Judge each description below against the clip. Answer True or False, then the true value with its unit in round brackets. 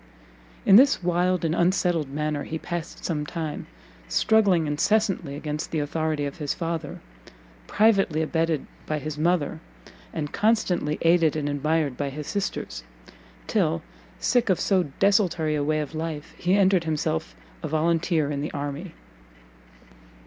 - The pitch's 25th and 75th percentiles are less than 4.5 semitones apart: True (3.1 semitones)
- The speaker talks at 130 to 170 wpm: True (140 wpm)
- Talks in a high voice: False (160 Hz)